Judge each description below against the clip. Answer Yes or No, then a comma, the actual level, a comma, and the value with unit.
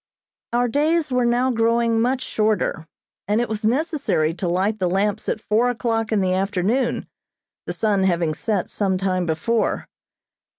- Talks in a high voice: Yes, high, 220 Hz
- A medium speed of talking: Yes, average, 160 wpm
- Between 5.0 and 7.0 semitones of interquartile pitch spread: No, average, 4.2 semitones